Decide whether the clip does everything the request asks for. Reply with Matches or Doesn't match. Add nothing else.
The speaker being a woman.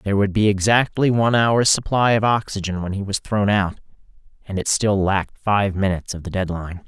Doesn't match